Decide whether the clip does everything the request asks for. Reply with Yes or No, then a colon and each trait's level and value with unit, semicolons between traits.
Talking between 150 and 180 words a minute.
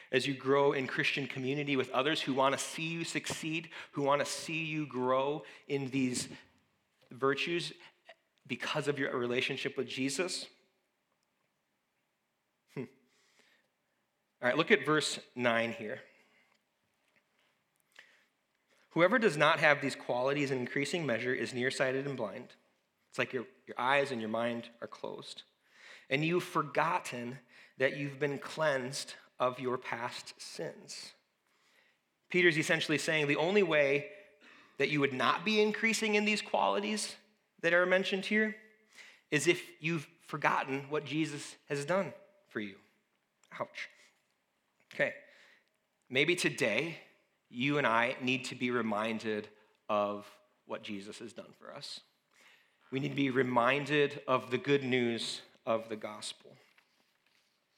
No: slow, 135 wpm